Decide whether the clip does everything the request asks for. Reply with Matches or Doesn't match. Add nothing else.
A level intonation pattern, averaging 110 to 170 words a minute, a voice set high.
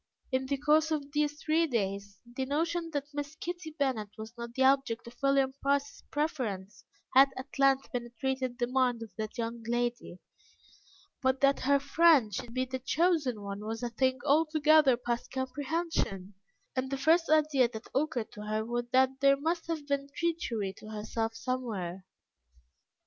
Doesn't match